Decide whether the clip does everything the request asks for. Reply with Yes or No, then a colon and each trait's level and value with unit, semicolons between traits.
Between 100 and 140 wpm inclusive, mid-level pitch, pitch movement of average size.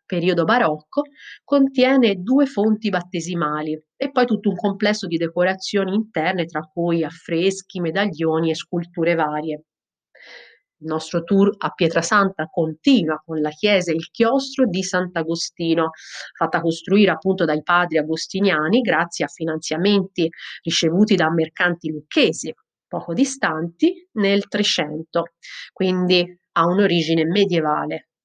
Yes: average, 120 wpm; medium, 175 Hz; average, 3.8 semitones